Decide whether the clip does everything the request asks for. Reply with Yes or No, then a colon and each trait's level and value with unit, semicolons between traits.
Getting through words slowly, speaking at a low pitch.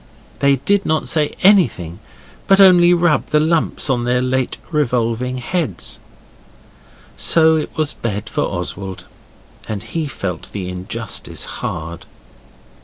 Yes: slow, 125 wpm; low, 130 Hz